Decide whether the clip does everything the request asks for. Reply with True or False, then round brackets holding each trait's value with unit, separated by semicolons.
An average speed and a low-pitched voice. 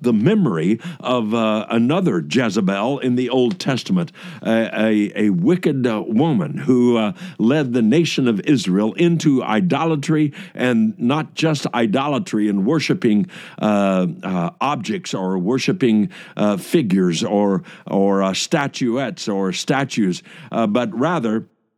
False (125 wpm; 125 Hz)